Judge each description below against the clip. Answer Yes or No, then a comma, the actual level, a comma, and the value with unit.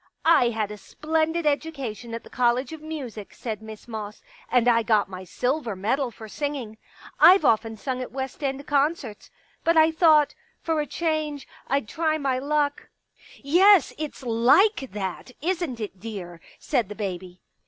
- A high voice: Yes, very high, 260 Hz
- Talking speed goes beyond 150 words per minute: Yes, average, 180 wpm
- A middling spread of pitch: No, wide, 5.9 semitones